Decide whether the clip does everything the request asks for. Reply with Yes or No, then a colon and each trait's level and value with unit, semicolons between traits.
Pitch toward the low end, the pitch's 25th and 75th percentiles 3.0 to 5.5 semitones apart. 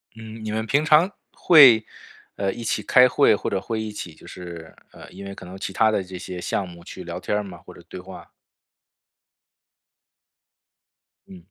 Yes: low, 100 Hz; average, 3.5 semitones